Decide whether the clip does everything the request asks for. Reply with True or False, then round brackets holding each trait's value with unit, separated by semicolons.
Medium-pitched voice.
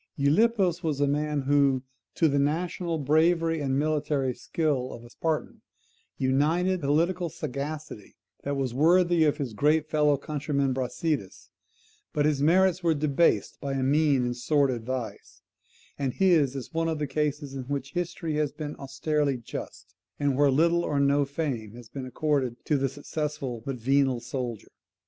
True (145 Hz)